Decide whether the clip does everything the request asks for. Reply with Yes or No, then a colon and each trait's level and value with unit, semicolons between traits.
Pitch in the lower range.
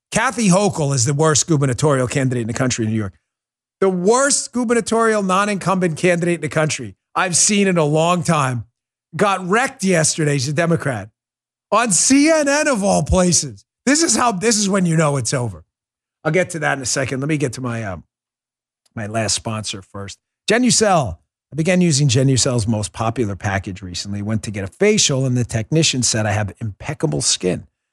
No: medium, 145 Hz